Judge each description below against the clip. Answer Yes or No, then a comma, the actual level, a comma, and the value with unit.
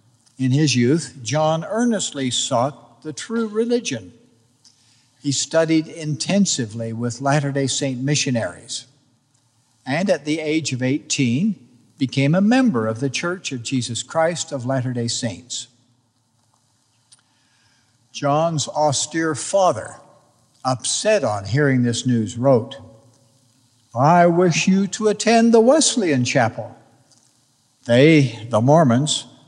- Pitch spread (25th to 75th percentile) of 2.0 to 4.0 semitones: No, average, 4.4 semitones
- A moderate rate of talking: No, slow, 115 wpm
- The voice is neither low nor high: No, low, 130 Hz